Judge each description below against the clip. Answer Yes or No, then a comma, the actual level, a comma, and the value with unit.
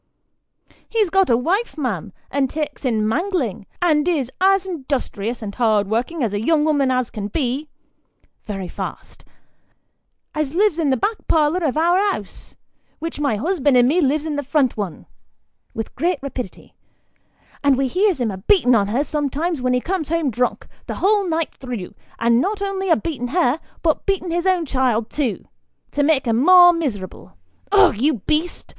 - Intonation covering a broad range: Yes, wide, 5.9 semitones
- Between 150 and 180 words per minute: Yes, average, 175 wpm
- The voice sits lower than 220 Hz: No, very high, 290 Hz